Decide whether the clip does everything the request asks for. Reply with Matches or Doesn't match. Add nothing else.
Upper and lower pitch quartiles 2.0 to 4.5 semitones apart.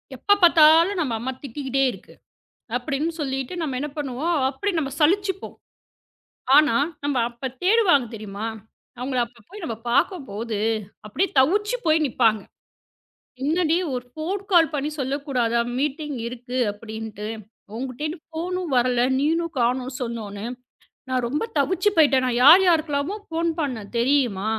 Doesn't match